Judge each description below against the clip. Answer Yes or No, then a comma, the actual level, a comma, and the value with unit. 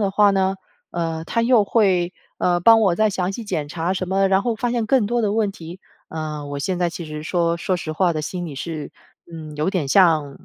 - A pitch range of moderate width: Yes, average, 3.9 semitones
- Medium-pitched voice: Yes, medium, 180 Hz